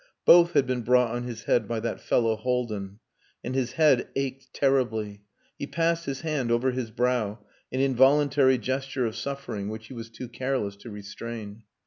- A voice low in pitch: Yes, low, 125 Hz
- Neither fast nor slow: Yes, average, 175 wpm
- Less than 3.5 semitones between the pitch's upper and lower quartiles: Yes, average, 3.0 semitones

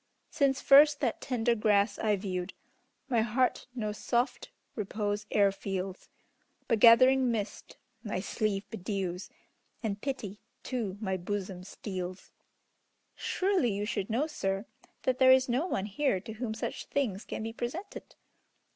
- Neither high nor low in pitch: No, high, 220 Hz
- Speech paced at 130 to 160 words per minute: Yes, average, 140 wpm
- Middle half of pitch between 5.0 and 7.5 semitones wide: No, average, 4.4 semitones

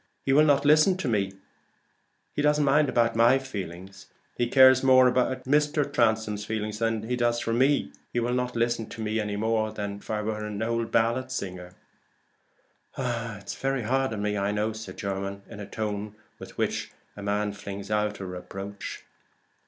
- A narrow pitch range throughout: No, average, 3.8 semitones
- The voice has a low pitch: Yes, low, 110 Hz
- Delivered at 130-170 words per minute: No, average, 180 wpm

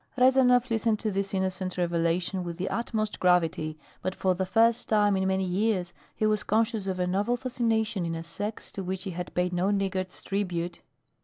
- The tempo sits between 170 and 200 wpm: Yes, average, 190 wpm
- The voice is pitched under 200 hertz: Yes, high, 190 Hz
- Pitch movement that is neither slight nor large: Yes, average, 3.3 semitones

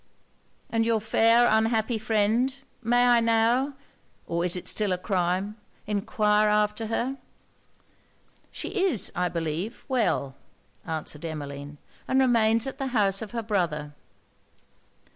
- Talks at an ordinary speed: No, slow, 125 wpm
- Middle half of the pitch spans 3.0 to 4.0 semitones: No, average, 4.4 semitones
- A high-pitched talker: Yes, high, 215 Hz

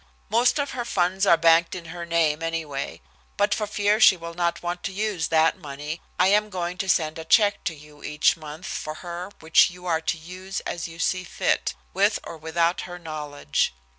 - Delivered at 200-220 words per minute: Yes, fast, 205 wpm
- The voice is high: No, medium, 170 Hz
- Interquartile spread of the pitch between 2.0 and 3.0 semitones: Yes, narrow, 2.6 semitones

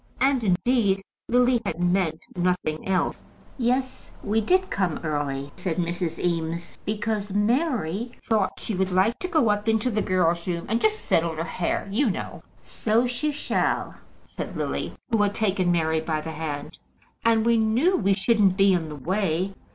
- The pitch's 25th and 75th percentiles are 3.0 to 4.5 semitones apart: No, average, 5.1 semitones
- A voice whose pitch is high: Yes, high, 195 Hz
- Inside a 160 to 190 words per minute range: Yes, average, 170 wpm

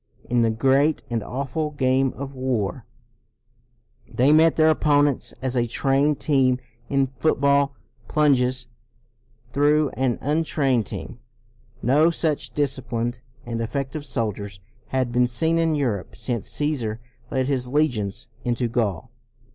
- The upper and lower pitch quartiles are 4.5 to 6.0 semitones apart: No, average, 3.3 semitones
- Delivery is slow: Yes, slow, 125 wpm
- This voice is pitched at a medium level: No, low, 130 Hz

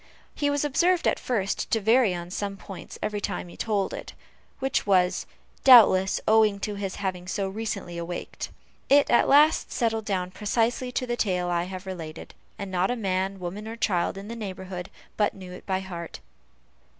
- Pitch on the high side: Yes, high, 200 Hz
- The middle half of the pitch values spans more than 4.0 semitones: No, average, 3.5 semitones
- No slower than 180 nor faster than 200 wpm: Yes, average, 185 wpm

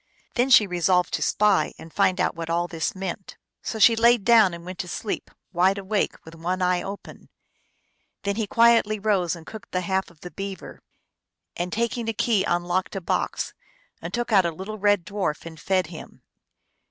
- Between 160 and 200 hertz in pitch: Yes, high, 190 Hz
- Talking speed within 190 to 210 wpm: Yes, average, 200 wpm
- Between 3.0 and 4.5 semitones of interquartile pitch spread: Yes, average, 3.4 semitones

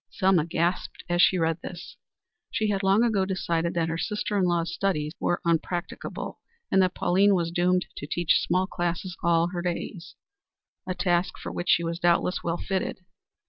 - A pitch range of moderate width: No, narrow, 1.9 semitones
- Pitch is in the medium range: Yes, medium, 175 Hz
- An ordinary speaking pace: Yes, average, 180 wpm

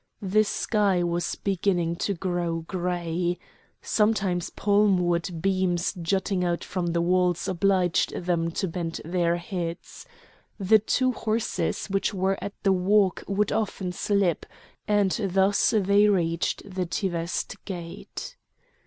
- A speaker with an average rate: No, slow, 125 wpm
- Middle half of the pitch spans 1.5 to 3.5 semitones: Yes, narrow, 2.5 semitones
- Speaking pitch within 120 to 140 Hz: No, medium, 185 Hz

